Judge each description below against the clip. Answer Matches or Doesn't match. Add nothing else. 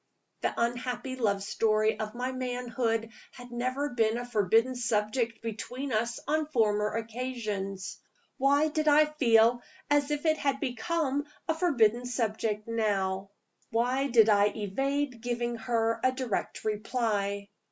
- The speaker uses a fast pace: Doesn't match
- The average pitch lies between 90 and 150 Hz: Doesn't match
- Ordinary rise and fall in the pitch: Matches